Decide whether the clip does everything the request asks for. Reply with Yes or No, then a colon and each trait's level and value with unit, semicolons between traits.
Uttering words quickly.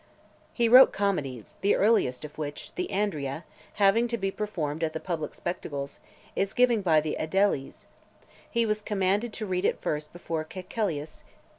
No: average, 155 wpm